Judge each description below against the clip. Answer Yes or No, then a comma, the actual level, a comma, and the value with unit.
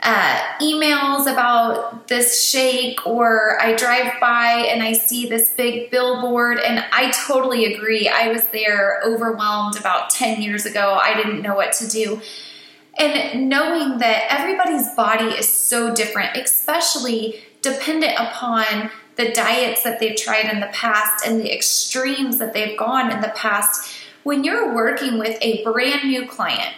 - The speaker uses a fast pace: No, average, 155 wpm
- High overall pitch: Yes, high, 235 Hz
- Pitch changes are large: No, narrow, 2.5 semitones